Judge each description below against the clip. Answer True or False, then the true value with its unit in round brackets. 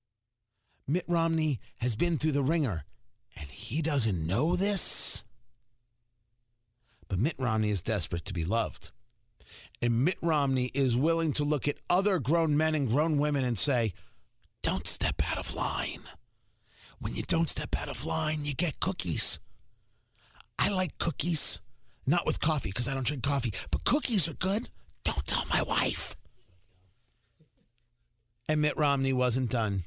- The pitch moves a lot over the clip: True (5.8 semitones)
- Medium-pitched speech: False (125 Hz)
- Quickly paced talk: False (150 wpm)